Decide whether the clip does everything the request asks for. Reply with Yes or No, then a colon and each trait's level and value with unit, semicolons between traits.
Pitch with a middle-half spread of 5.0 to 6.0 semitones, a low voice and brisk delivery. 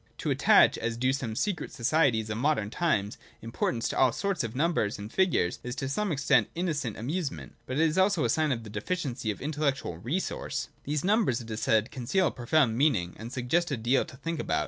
Yes: wide, 5.6 semitones; low, 130 Hz; fast, 215 wpm